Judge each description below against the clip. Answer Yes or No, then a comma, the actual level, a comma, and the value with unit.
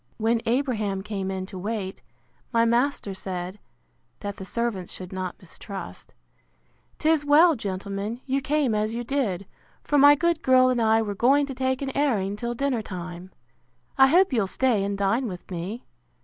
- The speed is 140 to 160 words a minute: No, average, 170 wpm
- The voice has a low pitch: No, high, 225 Hz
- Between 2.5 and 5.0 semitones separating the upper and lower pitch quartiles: No, wide, 5.4 semitones